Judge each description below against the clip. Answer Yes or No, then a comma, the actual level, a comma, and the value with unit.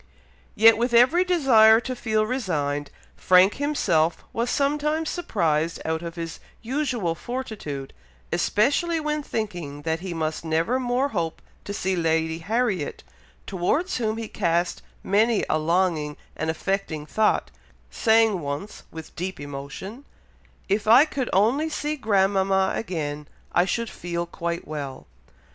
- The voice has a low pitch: No, high, 195 Hz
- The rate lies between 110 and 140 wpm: Yes, slow, 135 wpm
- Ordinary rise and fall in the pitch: No, wide, 6.9 semitones